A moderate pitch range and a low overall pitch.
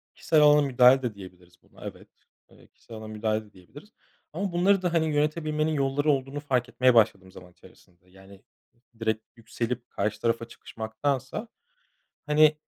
No: wide, 5.7 semitones; low, 125 Hz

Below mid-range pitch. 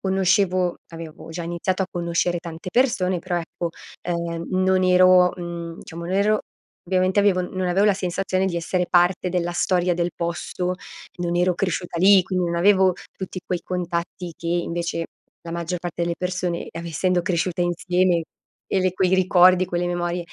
No: medium, 180 Hz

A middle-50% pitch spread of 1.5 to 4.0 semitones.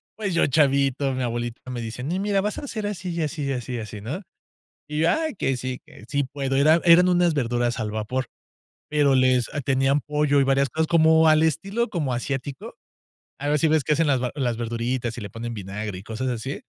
No: average, 4.7 semitones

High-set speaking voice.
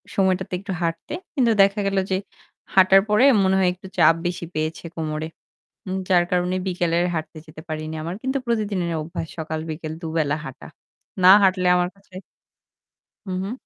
No: medium, 180 Hz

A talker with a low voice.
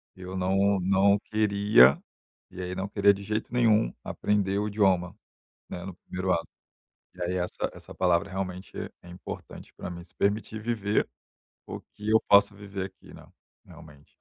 Yes: very low, 95 Hz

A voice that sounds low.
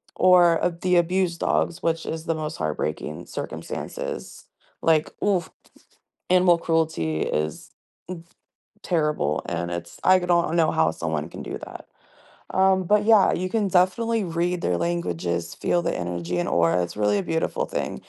No: medium, 165 Hz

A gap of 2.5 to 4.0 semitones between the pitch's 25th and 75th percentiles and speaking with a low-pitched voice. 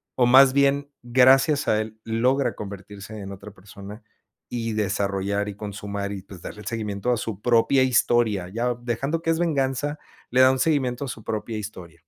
No: average, 4.4 semitones; low, 115 Hz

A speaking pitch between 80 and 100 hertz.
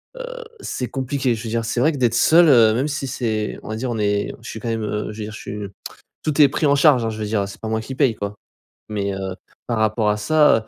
No: low, 115 Hz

